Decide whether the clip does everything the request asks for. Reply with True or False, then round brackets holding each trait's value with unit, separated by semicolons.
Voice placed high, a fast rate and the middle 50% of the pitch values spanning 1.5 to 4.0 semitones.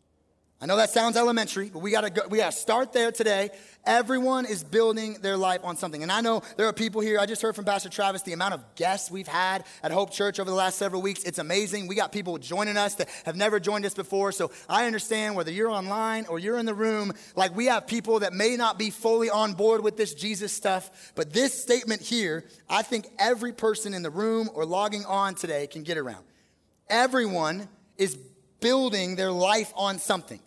True (205 Hz; 220 wpm; 2.8 semitones)